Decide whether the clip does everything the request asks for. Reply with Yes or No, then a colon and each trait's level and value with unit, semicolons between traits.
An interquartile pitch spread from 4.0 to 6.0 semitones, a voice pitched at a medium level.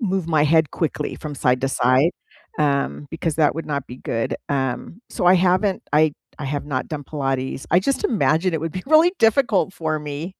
Yes: average, 4.4 semitones; medium, 155 Hz